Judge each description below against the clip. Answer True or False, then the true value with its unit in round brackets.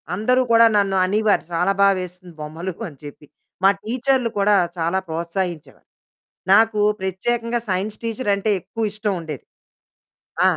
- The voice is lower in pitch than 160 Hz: False (195 Hz)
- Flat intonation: False (4.0 semitones)